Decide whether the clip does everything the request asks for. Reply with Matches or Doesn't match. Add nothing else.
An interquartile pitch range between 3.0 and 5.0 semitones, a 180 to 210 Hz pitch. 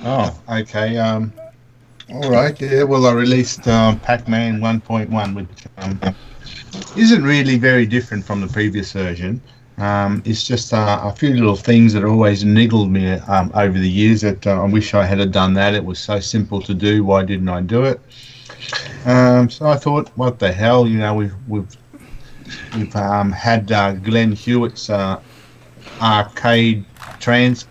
Doesn't match